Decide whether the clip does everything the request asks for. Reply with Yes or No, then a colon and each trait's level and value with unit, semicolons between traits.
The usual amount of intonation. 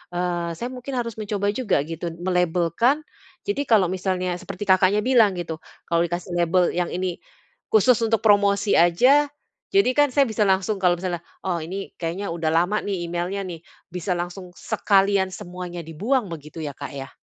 Yes: average, 3.5 semitones